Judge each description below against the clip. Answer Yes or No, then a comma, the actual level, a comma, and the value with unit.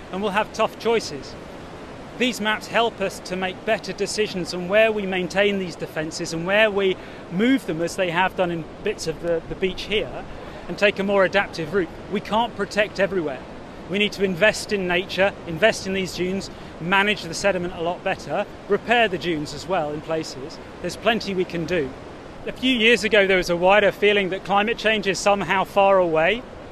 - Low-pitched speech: No, high, 195 Hz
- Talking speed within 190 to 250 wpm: Yes, average, 200 wpm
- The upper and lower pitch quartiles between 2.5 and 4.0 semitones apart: Yes, average, 2.8 semitones